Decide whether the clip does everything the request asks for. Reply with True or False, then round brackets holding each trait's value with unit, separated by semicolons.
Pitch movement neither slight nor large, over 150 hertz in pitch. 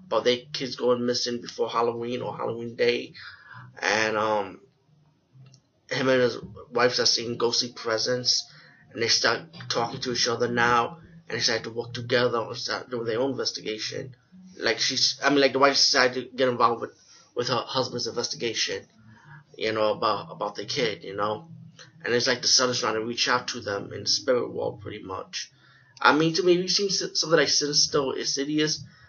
False (3.8 semitones; 125 Hz)